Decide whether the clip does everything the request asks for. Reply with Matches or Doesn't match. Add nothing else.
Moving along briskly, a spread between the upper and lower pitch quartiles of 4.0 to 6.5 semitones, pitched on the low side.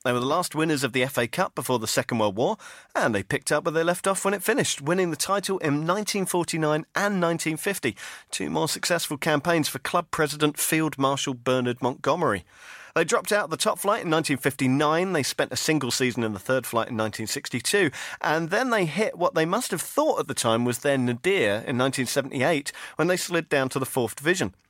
Doesn't match